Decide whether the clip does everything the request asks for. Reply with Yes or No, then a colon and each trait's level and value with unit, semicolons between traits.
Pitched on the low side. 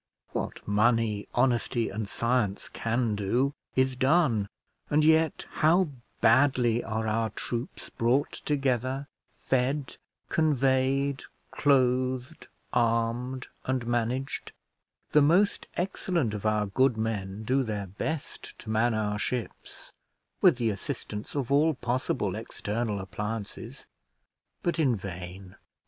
Yes: low, 120 Hz